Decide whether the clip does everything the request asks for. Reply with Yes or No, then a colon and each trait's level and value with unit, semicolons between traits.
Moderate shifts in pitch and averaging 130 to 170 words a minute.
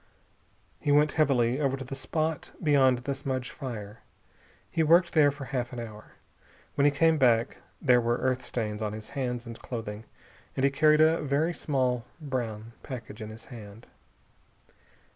Yes: average, 3.7 semitones; average, 165 wpm